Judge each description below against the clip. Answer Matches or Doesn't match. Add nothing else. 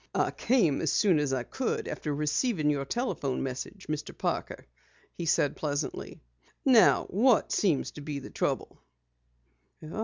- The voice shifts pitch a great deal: Matches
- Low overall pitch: Doesn't match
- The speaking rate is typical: Matches